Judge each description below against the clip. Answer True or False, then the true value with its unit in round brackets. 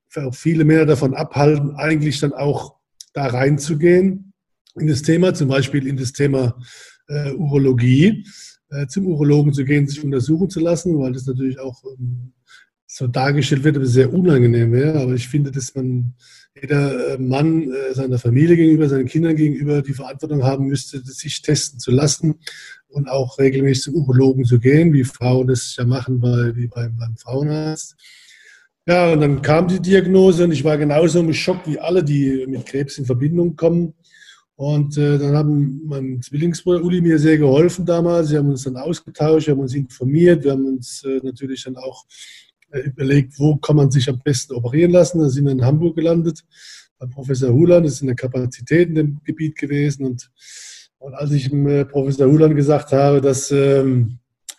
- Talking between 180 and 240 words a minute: True (185 wpm)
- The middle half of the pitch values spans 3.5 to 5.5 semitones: False (2.9 semitones)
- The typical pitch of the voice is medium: True (145 Hz)